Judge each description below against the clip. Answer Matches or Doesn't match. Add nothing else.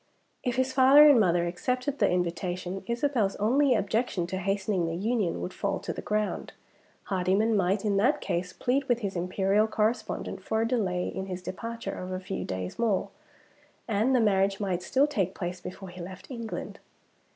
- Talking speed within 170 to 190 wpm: Matches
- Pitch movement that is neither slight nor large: Matches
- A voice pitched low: Doesn't match